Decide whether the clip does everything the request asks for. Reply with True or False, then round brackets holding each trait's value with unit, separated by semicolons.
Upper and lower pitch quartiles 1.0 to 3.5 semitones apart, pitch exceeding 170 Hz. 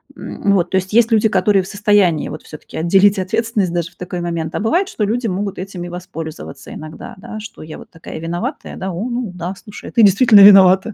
True (3.2 semitones; 190 Hz)